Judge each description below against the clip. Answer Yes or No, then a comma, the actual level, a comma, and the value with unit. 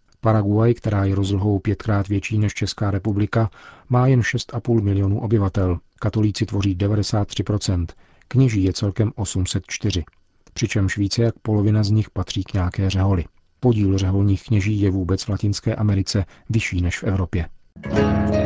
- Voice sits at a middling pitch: No, low, 100 Hz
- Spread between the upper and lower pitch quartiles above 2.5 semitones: No, narrow, 2.1 semitones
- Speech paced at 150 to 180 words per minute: No, average, 140 wpm